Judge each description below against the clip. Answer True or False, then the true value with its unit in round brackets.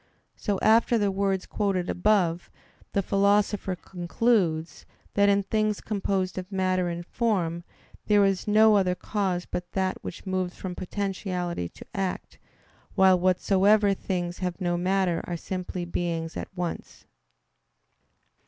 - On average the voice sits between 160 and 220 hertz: True (190 Hz)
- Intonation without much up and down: True (2.2 semitones)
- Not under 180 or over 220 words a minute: False (135 wpm)